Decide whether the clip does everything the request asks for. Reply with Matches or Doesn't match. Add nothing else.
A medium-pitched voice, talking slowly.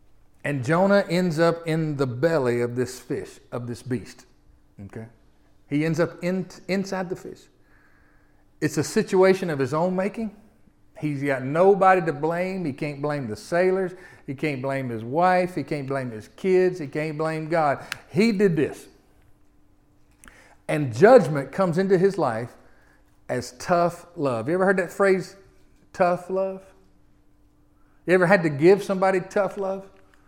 Doesn't match